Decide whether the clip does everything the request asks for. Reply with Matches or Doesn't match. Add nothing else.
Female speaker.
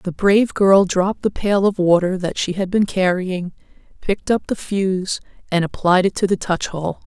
Matches